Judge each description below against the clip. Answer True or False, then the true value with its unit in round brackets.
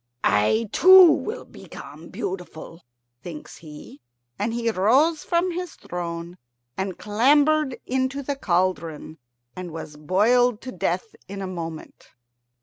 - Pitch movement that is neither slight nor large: False (8.5 semitones)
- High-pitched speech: True (205 Hz)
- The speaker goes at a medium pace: False (125 wpm)